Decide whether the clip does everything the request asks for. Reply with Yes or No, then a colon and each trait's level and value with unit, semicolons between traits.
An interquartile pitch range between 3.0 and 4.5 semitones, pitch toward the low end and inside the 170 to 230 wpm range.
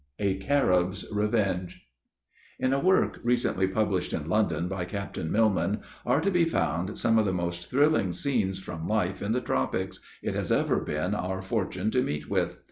Yes: average, 4.0 semitones; very low, 95 Hz; average, 175 wpm